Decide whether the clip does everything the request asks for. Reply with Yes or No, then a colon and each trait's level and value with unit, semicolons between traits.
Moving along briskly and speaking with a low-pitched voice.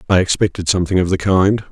Yes: fast, 210 wpm; very low, 95 Hz